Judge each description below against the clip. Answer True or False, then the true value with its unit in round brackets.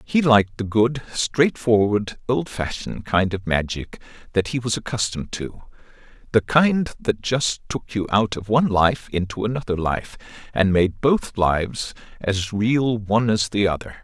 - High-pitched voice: False (110 Hz)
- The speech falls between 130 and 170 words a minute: True (155 wpm)